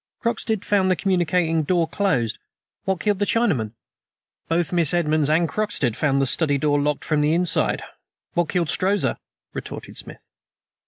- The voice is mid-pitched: Yes, medium, 165 Hz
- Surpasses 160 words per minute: No, average, 155 wpm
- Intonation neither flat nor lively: Yes, average, 4.1 semitones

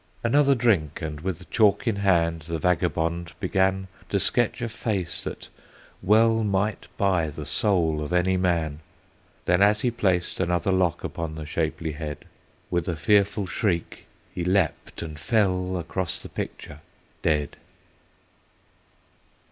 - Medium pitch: No, very low, 90 Hz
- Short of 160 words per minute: Yes, average, 140 wpm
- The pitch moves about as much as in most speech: Yes, average, 3.6 semitones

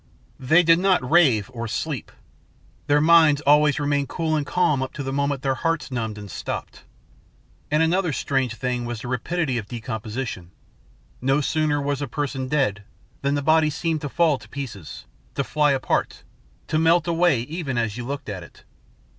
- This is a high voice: No, medium, 140 Hz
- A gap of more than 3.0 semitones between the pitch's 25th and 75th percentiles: Yes, average, 4.1 semitones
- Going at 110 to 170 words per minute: No, average, 180 wpm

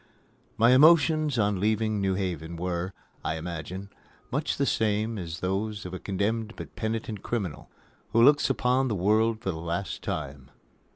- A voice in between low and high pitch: No, low, 100 Hz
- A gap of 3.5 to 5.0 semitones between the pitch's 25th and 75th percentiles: Yes, average, 4.0 semitones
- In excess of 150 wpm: Yes, average, 160 wpm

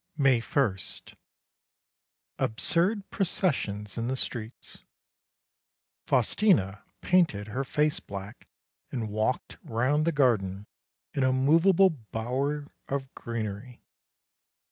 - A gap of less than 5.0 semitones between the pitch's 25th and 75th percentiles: No, wide, 5.6 semitones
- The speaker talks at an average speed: No, slow, 95 wpm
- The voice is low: Yes, low, 130 Hz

